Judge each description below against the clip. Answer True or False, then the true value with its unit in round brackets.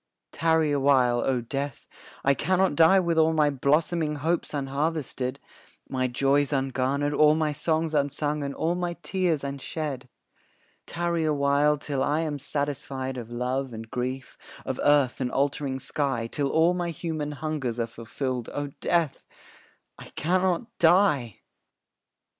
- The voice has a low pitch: False (145 Hz)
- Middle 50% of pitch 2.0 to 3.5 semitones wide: True (3.2 semitones)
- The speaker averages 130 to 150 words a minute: True (145 wpm)